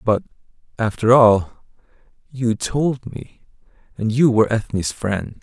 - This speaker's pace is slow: Yes, slow, 120 wpm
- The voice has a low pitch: Yes, low, 115 Hz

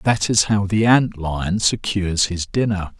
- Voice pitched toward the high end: No, low, 100 Hz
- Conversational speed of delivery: Yes, average, 180 wpm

